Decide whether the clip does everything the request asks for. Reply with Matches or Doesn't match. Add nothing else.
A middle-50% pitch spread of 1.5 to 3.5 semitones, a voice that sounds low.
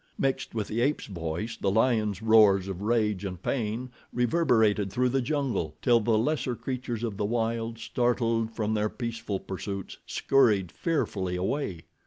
Matches